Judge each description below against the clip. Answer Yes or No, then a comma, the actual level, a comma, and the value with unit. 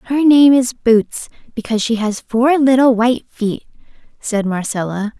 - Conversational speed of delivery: Yes, average, 150 wpm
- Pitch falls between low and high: No, high, 235 Hz